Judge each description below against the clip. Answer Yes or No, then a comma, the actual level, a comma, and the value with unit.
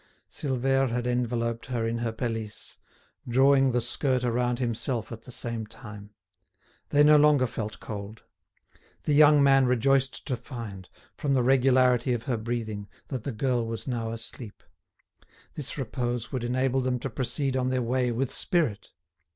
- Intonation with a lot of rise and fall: No, narrow, 2.5 semitones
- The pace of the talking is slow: No, average, 160 wpm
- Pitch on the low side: Yes, low, 125 Hz